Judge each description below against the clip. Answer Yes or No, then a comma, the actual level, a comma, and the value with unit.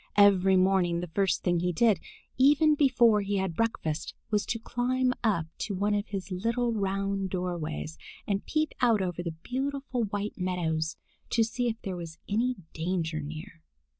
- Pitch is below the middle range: No, high, 195 Hz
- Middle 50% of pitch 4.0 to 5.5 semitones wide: Yes, average, 4.7 semitones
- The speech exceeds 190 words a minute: No, average, 165 wpm